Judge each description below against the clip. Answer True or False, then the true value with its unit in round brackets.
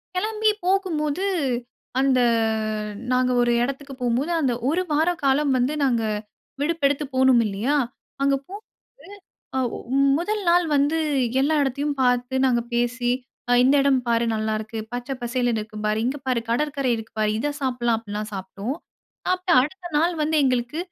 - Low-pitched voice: False (265 Hz)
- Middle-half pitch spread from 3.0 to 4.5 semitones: True (3.8 semitones)